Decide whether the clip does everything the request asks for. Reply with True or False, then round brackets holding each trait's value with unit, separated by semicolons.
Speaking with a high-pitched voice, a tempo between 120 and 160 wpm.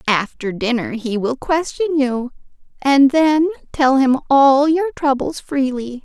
True (270 Hz; 140 wpm)